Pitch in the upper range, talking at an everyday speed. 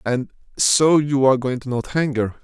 No: low, 135 Hz; average, 170 wpm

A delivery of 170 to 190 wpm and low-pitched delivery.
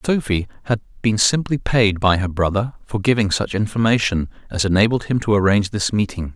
Yes: average, 180 wpm; low, 105 Hz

